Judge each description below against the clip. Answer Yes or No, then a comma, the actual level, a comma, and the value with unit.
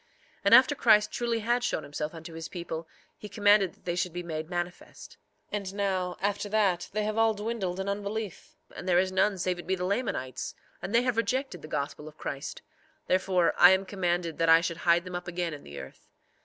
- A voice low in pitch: No, medium, 185 Hz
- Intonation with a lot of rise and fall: No, average, 3.5 semitones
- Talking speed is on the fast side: Yes, fast, 225 wpm